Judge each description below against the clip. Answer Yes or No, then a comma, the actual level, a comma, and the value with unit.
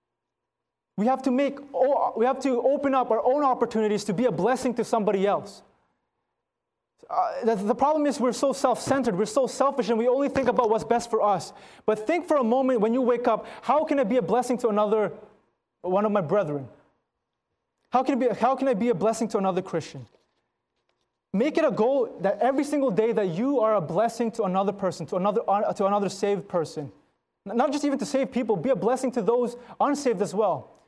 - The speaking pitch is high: Yes, high, 235 Hz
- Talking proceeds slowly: No, fast, 205 wpm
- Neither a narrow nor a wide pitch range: Yes, average, 3.8 semitones